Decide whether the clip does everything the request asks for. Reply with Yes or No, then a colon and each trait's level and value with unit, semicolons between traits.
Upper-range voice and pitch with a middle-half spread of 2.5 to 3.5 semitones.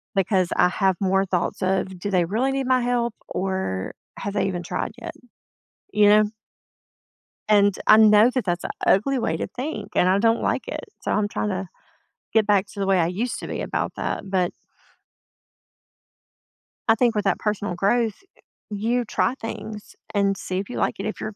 Yes: high, 205 Hz; average, 2.9 semitones